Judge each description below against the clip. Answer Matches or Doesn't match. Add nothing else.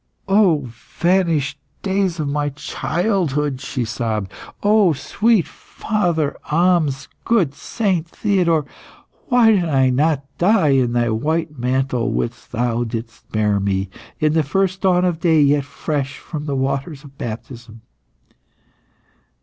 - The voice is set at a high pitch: Doesn't match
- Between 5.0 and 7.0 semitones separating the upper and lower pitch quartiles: Matches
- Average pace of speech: Doesn't match